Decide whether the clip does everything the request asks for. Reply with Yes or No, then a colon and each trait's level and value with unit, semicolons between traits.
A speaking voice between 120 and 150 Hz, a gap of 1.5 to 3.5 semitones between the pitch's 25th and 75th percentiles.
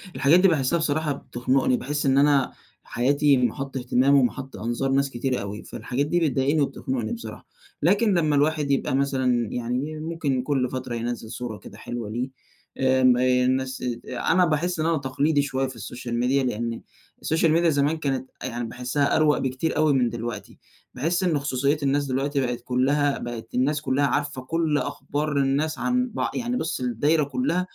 Yes: low, 135 Hz; average, 3.1 semitones